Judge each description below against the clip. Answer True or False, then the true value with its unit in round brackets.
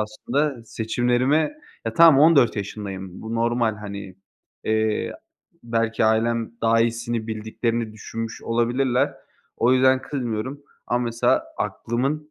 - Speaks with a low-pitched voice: True (115 Hz)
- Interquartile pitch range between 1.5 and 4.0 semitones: True (2.5 semitones)